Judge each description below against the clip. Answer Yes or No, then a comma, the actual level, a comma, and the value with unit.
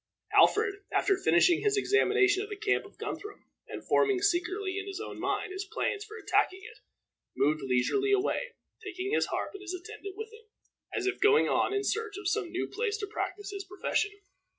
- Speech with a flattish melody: Yes, narrow, 1.8 semitones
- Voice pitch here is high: Yes, very high, 400 Hz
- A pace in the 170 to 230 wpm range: Yes, average, 195 wpm